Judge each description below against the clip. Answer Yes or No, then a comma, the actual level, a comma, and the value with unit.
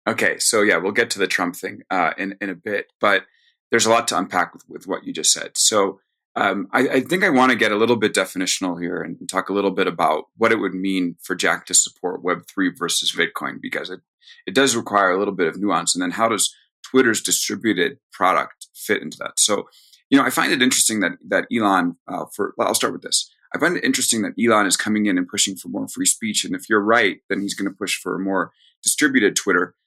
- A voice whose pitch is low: Yes, low, 110 Hz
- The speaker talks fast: Yes, fast, 250 wpm